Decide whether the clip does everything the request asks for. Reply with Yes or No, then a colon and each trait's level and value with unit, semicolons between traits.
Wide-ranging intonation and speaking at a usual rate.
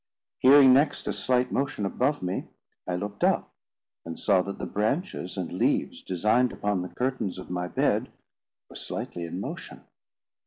Yes: wide, 5.9 semitones; average, 160 wpm